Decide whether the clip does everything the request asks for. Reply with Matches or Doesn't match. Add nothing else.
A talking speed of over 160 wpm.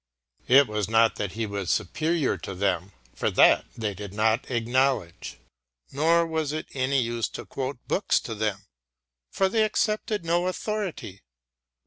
Doesn't match